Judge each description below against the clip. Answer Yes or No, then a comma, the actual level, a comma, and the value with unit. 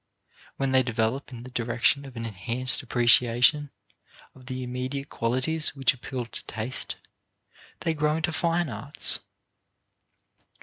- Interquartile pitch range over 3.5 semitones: No, average, 2.9 semitones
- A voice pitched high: No, low, 130 Hz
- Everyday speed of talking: No, slow, 130 wpm